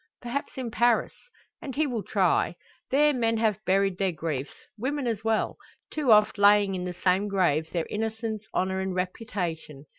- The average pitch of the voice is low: No, high, 210 Hz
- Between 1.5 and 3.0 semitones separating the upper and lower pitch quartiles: No, average, 3.8 semitones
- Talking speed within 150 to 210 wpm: Yes, average, 170 wpm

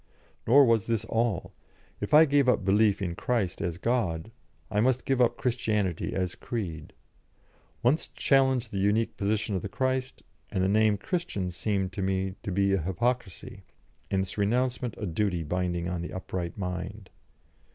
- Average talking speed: Yes, average, 165 wpm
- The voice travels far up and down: No, average, 4.5 semitones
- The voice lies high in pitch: No, low, 105 Hz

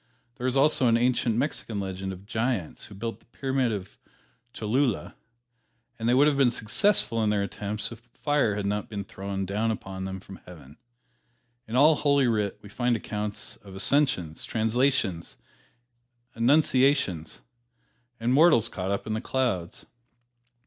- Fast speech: No, average, 155 wpm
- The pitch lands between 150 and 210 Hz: No, low, 110 Hz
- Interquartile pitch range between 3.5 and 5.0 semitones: Yes, average, 4.6 semitones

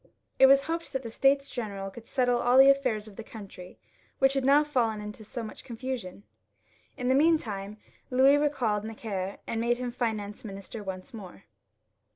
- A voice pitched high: Yes, high, 235 Hz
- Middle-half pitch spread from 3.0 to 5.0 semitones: Yes, average, 4.2 semitones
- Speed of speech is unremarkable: Yes, average, 180 wpm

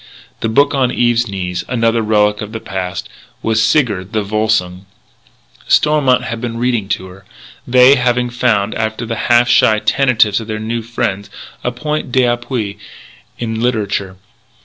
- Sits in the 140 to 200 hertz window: No, low, 115 Hz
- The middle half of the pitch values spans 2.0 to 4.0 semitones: Yes, average, 2.8 semitones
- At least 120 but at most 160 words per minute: Yes, average, 150 wpm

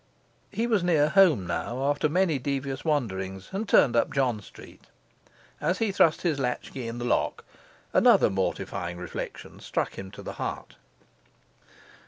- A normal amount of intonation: No, wide, 6.2 semitones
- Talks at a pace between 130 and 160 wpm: Yes, average, 150 wpm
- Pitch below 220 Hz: Yes, low, 135 Hz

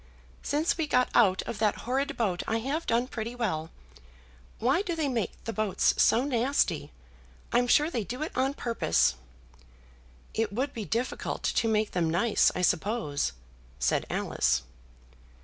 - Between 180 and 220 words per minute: No, average, 155 wpm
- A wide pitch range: No, average, 4.2 semitones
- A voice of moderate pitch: No, high, 235 Hz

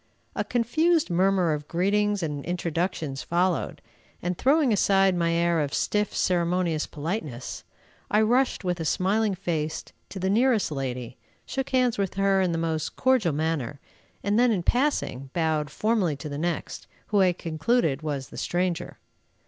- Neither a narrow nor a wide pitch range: Yes, average, 4.8 semitones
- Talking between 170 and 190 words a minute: No, average, 155 wpm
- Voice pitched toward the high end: No, medium, 180 Hz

